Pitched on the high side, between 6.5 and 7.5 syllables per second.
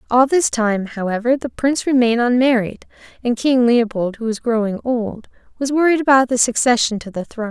No: high, 240 Hz; 5.6 syllables/s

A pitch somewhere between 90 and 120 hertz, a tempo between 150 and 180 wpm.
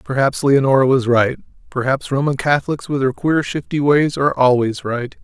No: low, 135 Hz; average, 170 wpm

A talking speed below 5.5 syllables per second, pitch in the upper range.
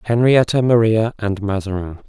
No: 4.8 syllables/s; low, 110 Hz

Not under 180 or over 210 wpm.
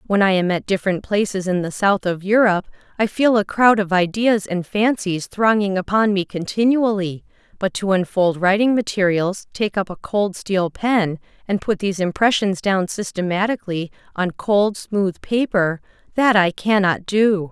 No: average, 160 wpm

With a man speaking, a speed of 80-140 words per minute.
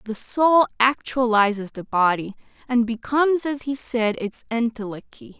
No: female; slow, 135 wpm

